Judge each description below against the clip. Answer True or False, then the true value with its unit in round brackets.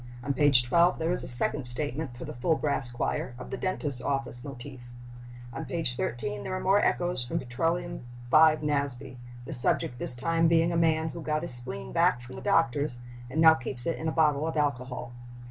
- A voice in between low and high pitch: True (145 Hz)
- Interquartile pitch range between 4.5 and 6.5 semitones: True (4.8 semitones)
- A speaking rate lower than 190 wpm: False (205 wpm)